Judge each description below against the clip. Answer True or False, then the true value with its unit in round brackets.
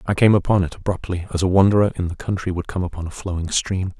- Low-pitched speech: True (90 Hz)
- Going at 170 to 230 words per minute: False (255 wpm)